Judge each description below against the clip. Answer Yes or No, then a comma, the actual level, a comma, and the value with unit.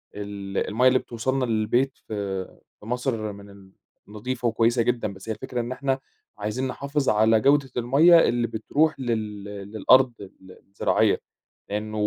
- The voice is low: Yes, low, 115 Hz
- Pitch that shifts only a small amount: No, average, 3.7 semitones